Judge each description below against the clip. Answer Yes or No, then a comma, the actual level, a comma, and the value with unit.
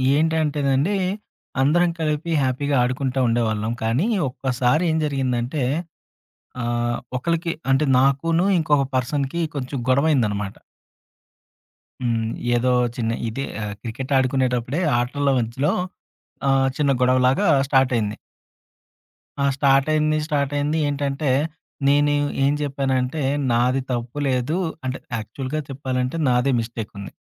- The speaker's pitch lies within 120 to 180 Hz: Yes, low, 135 Hz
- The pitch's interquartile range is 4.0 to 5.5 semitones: No, average, 2.9 semitones